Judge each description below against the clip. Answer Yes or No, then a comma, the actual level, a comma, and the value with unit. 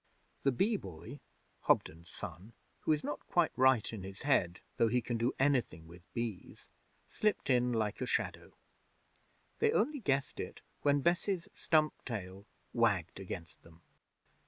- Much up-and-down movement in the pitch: Yes, wide, 7.3 semitones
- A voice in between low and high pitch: No, low, 120 Hz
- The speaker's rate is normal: Yes, average, 150 wpm